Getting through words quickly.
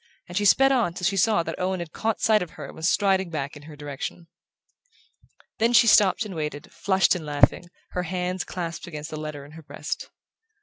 Yes: fast, 215 wpm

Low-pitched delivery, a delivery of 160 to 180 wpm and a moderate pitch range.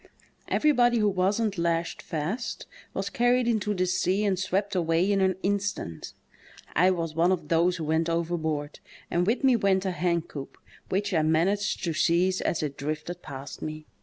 No: medium, 180 Hz; average, 170 wpm; average, 3.7 semitones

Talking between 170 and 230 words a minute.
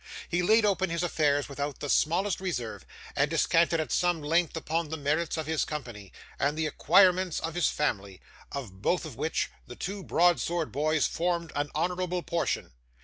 Yes: average, 180 wpm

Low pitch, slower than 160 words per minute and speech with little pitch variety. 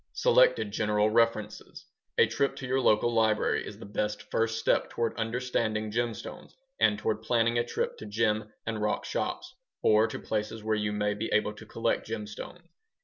No: low, 110 Hz; average, 175 wpm; narrow, 1.7 semitones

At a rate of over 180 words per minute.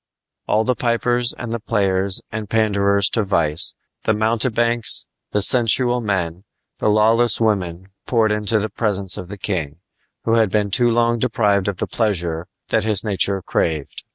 No: average, 165 wpm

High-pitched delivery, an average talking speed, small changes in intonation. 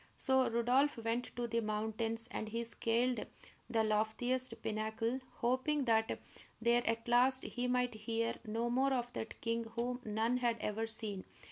Yes: high, 235 Hz; average, 155 wpm; narrow, 1.8 semitones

